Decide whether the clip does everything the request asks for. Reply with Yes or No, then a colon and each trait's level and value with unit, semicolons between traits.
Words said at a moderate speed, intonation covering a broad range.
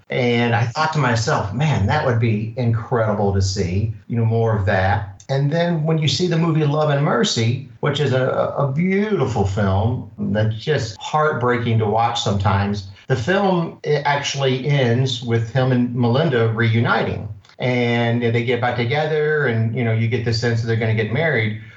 No: average, 185 wpm; average, 4.3 semitones